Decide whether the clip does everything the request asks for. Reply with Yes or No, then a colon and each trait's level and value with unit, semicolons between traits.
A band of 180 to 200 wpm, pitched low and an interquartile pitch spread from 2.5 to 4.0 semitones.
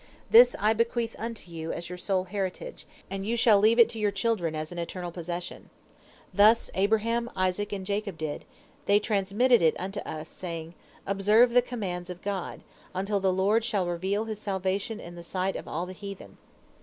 No: average, 185 wpm; high, 200 Hz; average, 3.5 semitones